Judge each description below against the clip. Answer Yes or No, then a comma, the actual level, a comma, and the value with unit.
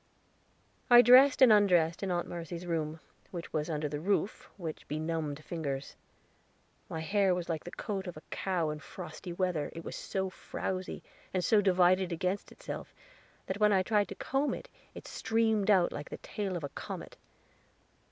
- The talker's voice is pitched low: No, medium, 180 Hz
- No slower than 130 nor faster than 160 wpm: No, average, 175 wpm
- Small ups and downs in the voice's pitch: No, average, 3.7 semitones